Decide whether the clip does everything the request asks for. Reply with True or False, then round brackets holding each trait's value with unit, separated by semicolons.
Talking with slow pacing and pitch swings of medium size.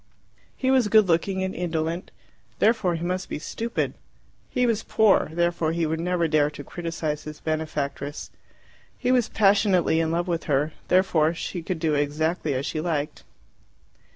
False (160 wpm; 3.3 semitones)